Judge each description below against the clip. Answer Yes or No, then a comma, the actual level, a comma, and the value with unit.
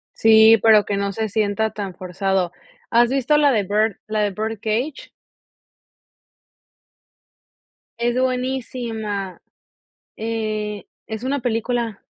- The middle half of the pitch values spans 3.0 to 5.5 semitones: No, narrow, 2.6 semitones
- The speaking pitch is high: Yes, high, 220 Hz